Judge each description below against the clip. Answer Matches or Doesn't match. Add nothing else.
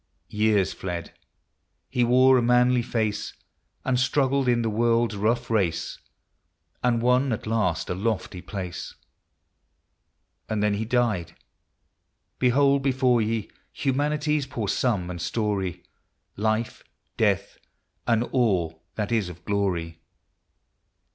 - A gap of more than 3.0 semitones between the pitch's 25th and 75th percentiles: Matches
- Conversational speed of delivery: Doesn't match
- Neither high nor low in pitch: Doesn't match